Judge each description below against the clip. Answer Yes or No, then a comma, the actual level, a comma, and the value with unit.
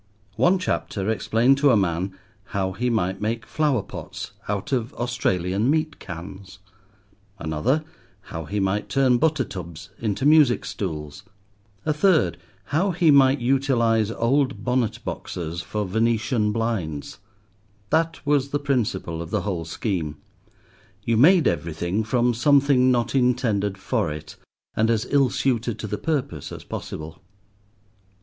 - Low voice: Yes, low, 115 Hz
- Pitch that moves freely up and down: Yes, wide, 6.2 semitones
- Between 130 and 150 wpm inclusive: Yes, average, 140 wpm